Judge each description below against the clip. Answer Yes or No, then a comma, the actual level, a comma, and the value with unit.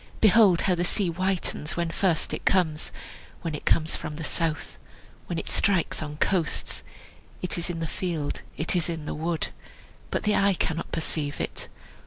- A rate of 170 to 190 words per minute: Yes, average, 180 wpm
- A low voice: No, medium, 170 Hz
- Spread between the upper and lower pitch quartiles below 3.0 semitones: Yes, narrow, 2.6 semitones